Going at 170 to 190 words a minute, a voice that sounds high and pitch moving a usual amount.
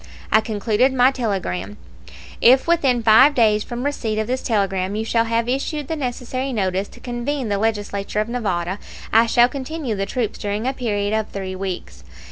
Yes: average, 180 wpm; high, 225 Hz; average, 3.8 semitones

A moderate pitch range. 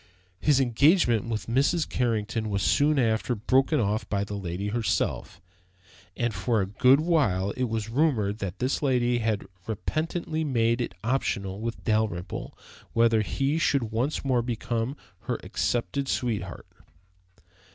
Yes: average, 3.9 semitones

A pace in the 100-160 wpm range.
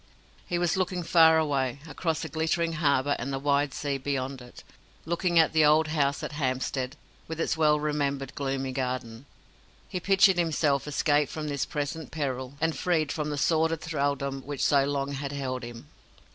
No: average, 175 wpm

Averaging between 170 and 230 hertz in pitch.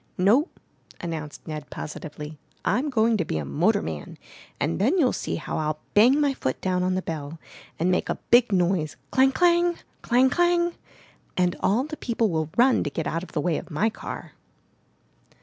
Yes: medium, 185 Hz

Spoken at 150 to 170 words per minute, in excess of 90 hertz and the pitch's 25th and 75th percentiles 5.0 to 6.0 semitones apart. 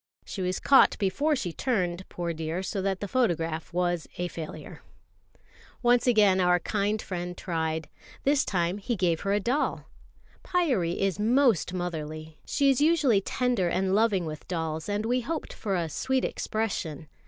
Yes: average, 160 wpm; high, 190 Hz; wide, 5.5 semitones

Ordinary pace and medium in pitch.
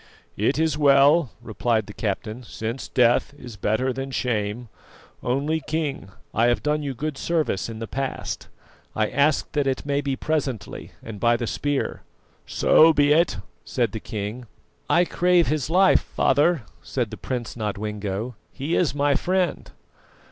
No: average, 155 wpm; low, 130 Hz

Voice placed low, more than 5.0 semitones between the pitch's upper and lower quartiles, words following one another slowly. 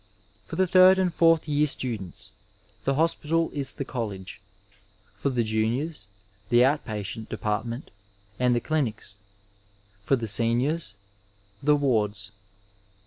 Yes: low, 125 Hz; wide, 5.6 semitones; slow, 130 wpm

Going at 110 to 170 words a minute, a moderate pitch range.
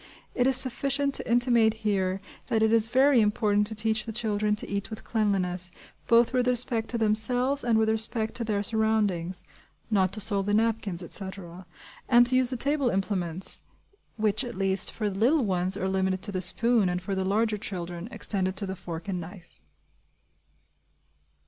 No: average, 180 wpm; average, 3.5 semitones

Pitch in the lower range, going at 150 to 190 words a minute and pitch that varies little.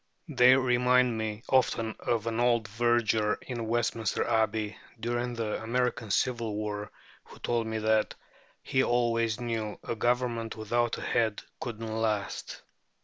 No: low, 115 Hz; average, 140 wpm; narrow, 1.7 semitones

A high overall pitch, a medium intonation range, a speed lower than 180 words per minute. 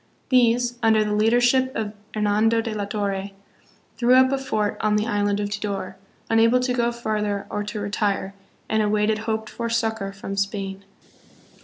No: high, 215 Hz; narrow, 2.2 semitones; average, 165 wpm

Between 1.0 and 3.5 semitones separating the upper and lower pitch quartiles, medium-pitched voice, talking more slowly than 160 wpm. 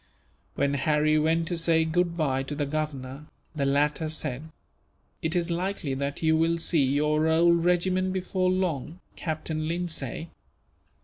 Yes: average, 2.7 semitones; medium, 160 Hz; average, 140 wpm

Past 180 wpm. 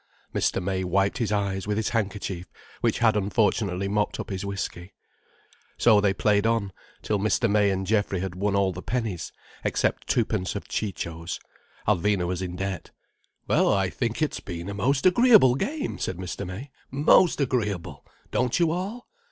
No: average, 170 wpm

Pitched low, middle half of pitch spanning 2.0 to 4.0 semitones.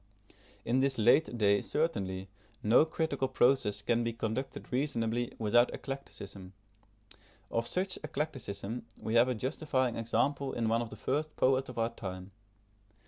Yes: low, 120 Hz; average, 3.5 semitones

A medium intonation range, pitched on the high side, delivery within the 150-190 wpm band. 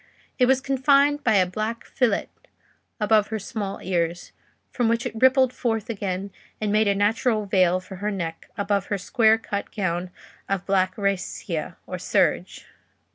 Yes: average, 3.2 semitones; high, 210 Hz; average, 160 wpm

